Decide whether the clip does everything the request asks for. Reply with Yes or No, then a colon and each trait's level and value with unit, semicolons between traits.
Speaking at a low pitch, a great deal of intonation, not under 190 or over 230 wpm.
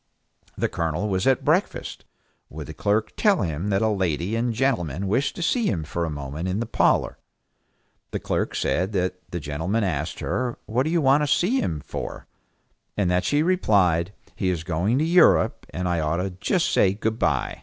Yes: very low, 95 Hz; wide, 6.3 semitones; average, 195 wpm